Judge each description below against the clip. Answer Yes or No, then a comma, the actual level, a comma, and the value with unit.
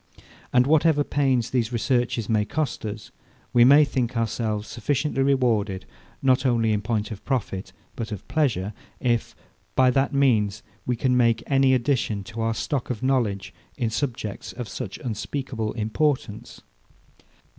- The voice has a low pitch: Yes, low, 120 Hz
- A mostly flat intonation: No, average, 3.6 semitones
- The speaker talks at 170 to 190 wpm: No, average, 145 wpm